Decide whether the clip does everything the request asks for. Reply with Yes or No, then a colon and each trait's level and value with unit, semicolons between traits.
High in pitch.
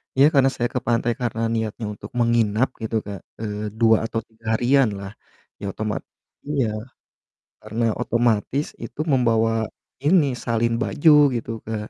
No: low, 115 Hz